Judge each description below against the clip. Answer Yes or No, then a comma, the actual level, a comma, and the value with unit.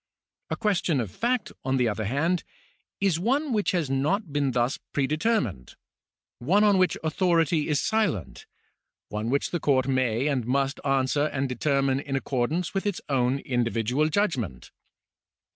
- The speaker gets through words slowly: No, average, 160 wpm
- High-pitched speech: No, medium, 140 Hz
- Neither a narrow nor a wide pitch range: No, wide, 5.7 semitones